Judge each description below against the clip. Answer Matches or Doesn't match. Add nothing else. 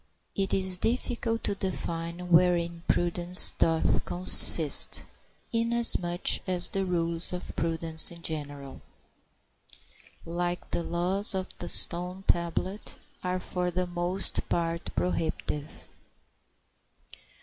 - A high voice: Doesn't match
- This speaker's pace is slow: Matches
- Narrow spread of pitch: Matches